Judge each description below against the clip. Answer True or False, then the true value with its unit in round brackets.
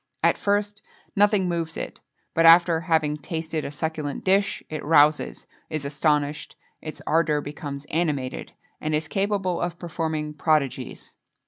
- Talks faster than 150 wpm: False (135 wpm)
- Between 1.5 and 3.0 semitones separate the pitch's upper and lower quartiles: True (2.5 semitones)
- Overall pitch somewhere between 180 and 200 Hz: False (160 Hz)